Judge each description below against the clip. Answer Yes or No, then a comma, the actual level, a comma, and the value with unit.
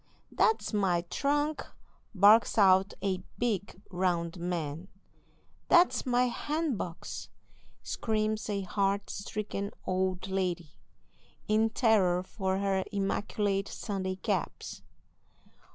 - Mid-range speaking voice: No, high, 195 Hz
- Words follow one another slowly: Yes, slow, 95 wpm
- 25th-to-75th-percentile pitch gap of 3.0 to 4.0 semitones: No, narrow, 2.6 semitones